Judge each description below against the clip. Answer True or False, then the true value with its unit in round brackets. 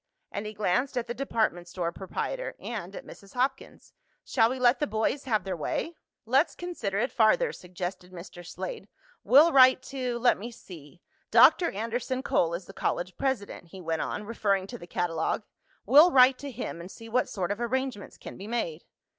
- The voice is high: True (225 Hz)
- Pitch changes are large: True (6.0 semitones)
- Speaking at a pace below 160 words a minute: False (190 wpm)